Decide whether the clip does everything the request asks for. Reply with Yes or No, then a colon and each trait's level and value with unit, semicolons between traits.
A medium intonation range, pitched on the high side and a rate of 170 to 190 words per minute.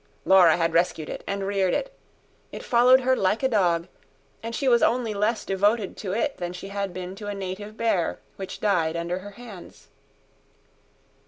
Yes: average, 3.8 semitones; high, 200 Hz; average, 180 wpm